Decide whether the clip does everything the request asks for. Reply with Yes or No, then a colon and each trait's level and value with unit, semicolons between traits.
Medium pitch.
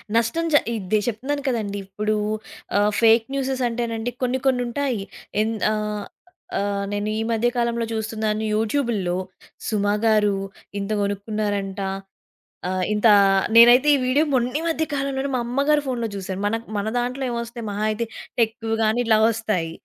No: high, 225 Hz